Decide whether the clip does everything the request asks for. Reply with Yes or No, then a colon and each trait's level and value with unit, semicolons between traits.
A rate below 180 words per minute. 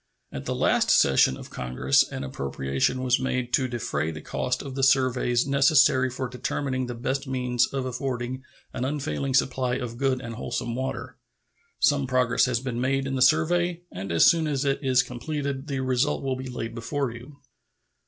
No: average, 185 wpm